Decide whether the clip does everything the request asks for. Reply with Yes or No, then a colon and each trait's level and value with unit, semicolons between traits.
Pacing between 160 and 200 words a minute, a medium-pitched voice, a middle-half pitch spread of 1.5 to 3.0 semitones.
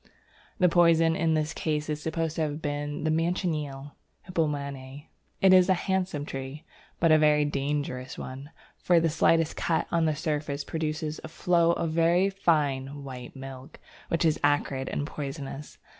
Yes: average, 165 wpm; medium, 155 Hz; narrow, 2.6 semitones